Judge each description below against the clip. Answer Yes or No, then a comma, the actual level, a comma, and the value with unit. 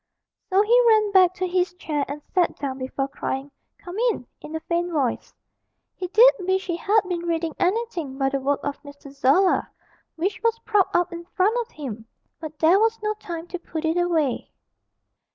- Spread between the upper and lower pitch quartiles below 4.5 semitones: No, average, 4.8 semitones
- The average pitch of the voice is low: No, very high, 350 Hz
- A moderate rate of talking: Yes, average, 190 wpm